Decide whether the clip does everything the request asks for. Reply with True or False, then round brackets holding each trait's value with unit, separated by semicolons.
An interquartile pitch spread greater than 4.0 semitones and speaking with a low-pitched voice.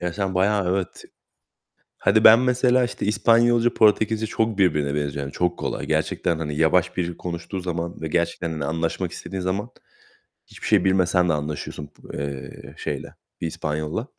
True (4.8 semitones; 90 Hz)